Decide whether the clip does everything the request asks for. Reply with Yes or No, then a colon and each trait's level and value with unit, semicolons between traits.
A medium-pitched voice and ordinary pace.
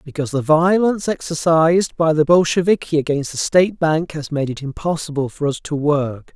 Yes: medium, 155 Hz; average, 180 wpm